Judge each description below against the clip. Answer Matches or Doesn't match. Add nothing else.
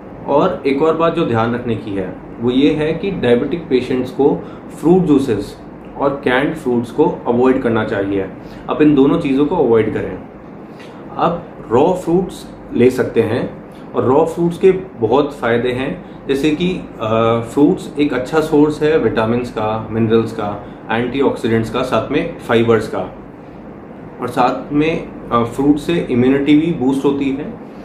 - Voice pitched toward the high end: Doesn't match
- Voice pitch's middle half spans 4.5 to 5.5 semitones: Matches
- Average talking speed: Matches